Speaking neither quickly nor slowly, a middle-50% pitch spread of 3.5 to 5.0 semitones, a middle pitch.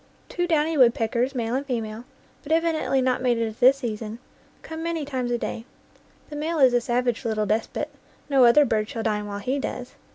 No: average, 195 wpm; average, 4.0 semitones; very high, 250 Hz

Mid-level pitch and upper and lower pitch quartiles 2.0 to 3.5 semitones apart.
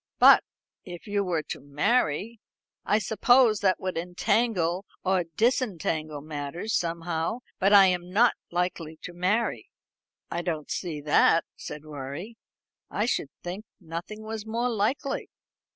No: medium, 180 Hz; average, 4.8 semitones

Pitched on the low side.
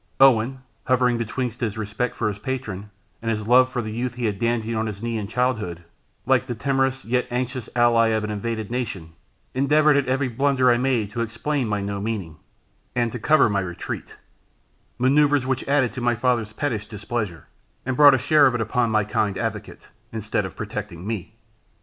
Yes: low, 120 Hz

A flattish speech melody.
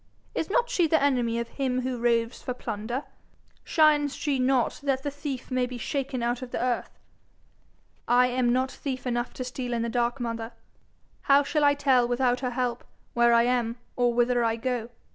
Yes: narrow, 2.2 semitones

